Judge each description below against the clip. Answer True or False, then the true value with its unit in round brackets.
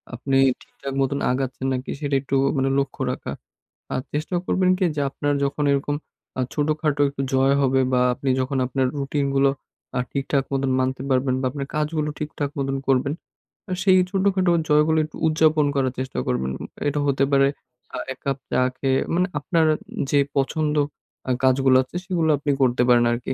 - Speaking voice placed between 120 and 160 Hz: True (140 Hz)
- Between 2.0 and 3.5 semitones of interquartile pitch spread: True (2.4 semitones)